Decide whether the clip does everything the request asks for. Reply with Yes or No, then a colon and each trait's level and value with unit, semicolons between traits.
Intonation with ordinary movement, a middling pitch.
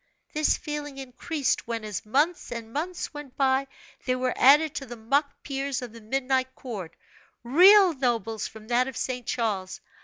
No: average, 3.8 semitones; very high, 260 Hz